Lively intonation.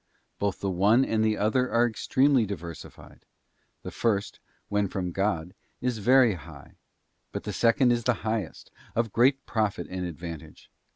No: average, 4.5 semitones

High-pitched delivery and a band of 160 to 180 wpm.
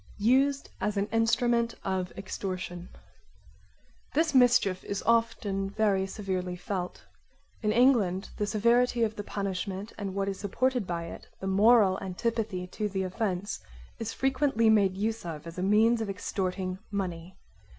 No: high, 200 Hz; average, 145 wpm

